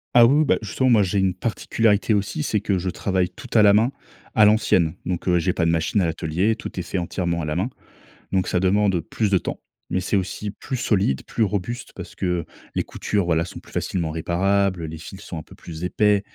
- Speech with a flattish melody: No, average, 3.3 semitones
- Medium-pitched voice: No, very low, 95 Hz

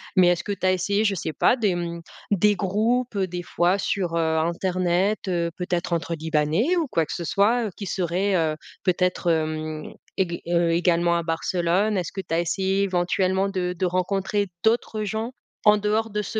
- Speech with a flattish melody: No, average, 3.0 semitones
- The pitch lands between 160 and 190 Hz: Yes, medium, 185 Hz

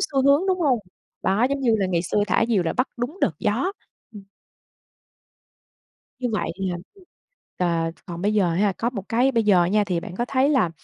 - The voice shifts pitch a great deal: Yes, wide, 5.9 semitones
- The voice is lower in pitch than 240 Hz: Yes, high, 210 Hz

